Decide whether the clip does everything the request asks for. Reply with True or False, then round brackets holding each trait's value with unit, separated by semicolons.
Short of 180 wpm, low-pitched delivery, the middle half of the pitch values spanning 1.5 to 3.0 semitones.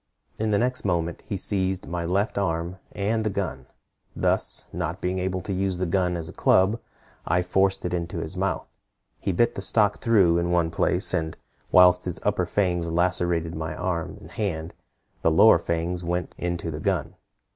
False (185 wpm; 90 Hz; 2.4 semitones)